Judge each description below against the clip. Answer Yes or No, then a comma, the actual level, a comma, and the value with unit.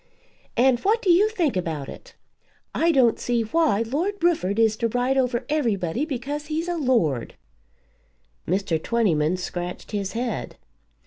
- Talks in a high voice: Yes, high, 240 Hz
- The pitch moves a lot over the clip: Yes, wide, 7.4 semitones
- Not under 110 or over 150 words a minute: Yes, average, 145 wpm